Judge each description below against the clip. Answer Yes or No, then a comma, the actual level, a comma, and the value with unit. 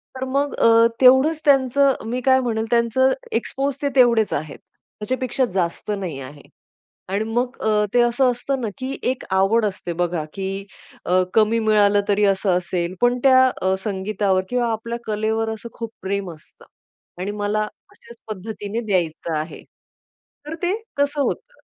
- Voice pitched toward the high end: Yes, high, 220 Hz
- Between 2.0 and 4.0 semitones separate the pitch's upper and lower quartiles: No, average, 4.7 semitones